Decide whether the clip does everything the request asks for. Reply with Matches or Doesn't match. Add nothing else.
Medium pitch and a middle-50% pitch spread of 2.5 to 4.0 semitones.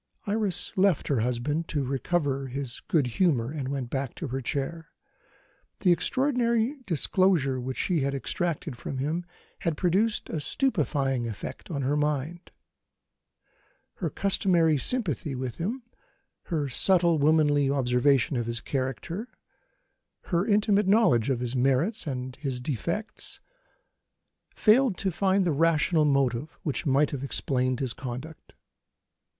Doesn't match